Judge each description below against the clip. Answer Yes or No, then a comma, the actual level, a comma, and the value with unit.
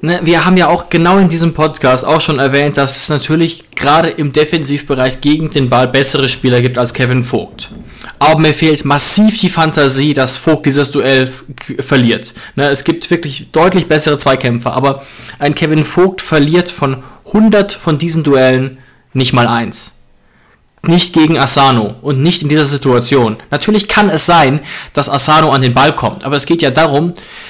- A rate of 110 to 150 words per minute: No, average, 175 wpm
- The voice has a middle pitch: Yes, medium, 145 Hz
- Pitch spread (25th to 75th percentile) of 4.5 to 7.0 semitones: No, average, 3.4 semitones